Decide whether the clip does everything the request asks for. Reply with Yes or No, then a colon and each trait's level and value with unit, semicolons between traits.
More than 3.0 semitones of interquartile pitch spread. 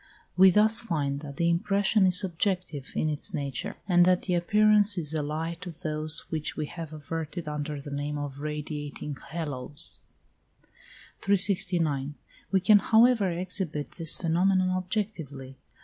Yes: average, 4.3 semitones